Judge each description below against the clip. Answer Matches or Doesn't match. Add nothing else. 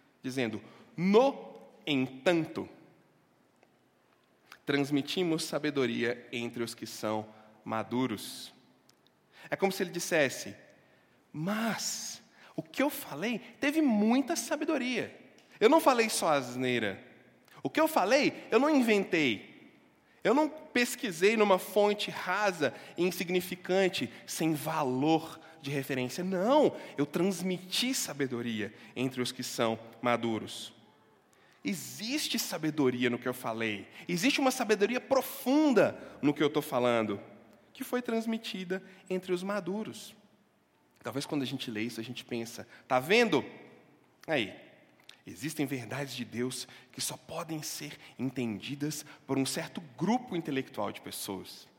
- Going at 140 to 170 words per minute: Doesn't match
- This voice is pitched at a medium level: Matches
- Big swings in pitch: Matches